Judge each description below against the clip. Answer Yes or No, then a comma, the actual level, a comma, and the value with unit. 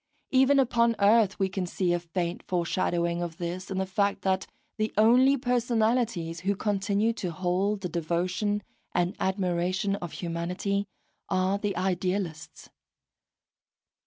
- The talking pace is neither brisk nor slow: No, slow, 130 wpm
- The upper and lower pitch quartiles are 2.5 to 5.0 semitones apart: Yes, average, 3.0 semitones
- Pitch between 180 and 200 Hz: Yes, high, 190 Hz